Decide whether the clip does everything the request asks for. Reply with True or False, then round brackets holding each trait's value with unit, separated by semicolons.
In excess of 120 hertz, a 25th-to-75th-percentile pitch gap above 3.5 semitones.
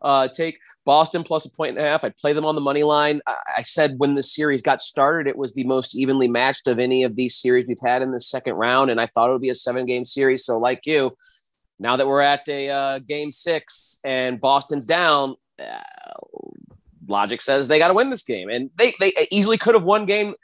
True (140 Hz; 4.2 semitones)